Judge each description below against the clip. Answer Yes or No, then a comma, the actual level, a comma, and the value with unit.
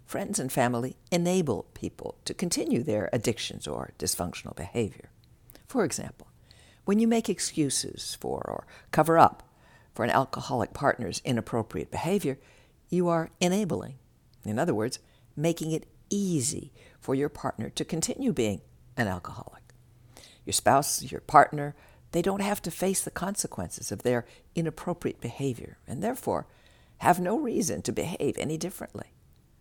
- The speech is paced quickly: No, average, 140 wpm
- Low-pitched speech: No, medium, 155 Hz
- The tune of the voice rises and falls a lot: Yes, wide, 6.5 semitones